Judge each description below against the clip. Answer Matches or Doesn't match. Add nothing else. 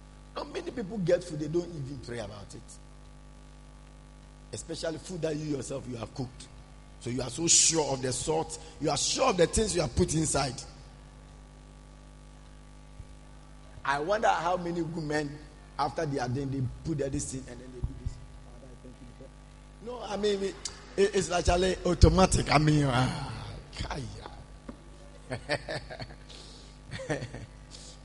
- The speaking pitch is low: Doesn't match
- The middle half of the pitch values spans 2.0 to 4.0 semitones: Doesn't match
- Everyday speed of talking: Matches